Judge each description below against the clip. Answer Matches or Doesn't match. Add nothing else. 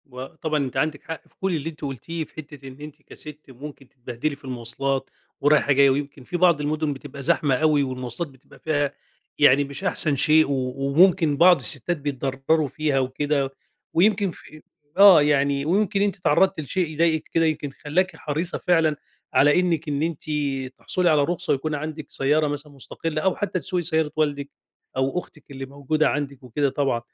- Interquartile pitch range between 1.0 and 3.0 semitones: Matches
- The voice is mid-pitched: Matches